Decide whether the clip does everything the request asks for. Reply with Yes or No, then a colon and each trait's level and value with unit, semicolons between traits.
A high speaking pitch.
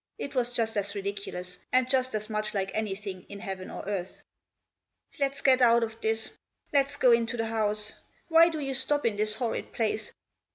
Yes: high, 225 Hz